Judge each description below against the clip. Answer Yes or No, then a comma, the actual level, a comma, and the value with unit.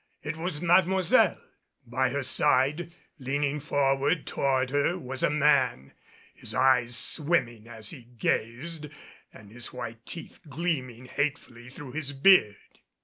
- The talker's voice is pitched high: No, low, 135 Hz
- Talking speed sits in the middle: No, slow, 130 wpm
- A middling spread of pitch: Yes, average, 3.7 semitones